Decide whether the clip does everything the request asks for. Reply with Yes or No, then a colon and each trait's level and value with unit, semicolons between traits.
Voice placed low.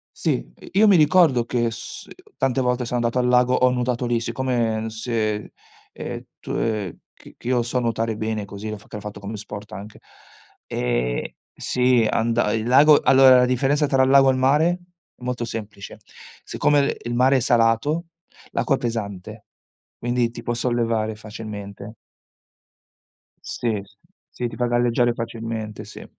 Yes: low, 120 Hz